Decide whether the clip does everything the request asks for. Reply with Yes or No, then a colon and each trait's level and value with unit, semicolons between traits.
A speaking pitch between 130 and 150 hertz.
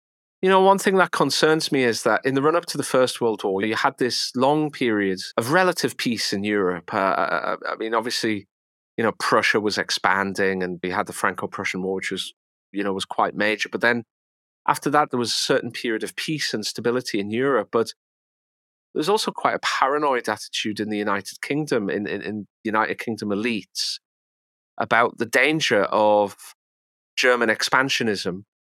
No: low, 110 Hz